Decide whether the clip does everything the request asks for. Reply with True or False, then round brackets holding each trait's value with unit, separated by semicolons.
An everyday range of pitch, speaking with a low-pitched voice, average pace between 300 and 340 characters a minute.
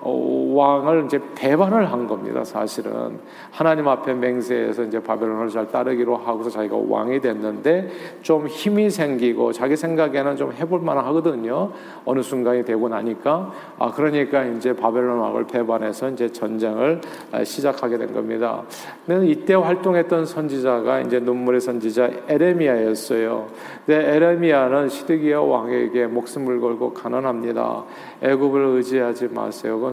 True (4.3 semitones; 130 Hz; 330 characters per minute)